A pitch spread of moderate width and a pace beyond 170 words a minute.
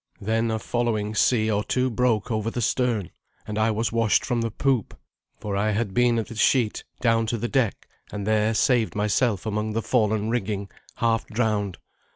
No: narrow, 1.9 semitones; average, 190 wpm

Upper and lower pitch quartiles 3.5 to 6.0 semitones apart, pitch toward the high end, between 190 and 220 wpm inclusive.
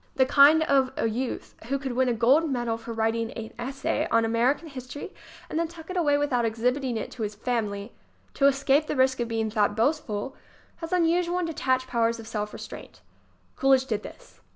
Yes: average, 4.0 semitones; very high, 255 Hz; fast, 205 wpm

